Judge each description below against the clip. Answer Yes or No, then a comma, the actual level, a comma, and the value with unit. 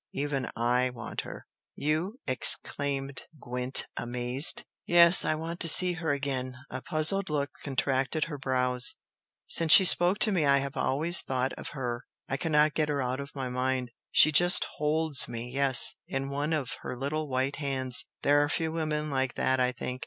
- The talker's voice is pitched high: No, medium, 140 Hz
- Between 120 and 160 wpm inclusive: No, average, 180 wpm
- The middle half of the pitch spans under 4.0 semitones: Yes, average, 3.3 semitones